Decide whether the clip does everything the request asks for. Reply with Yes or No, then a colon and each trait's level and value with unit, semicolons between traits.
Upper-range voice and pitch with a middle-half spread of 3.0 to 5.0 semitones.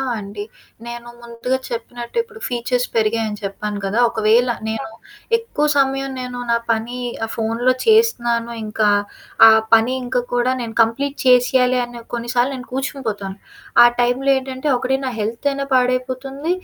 No: high, 245 Hz; narrow, 2.4 semitones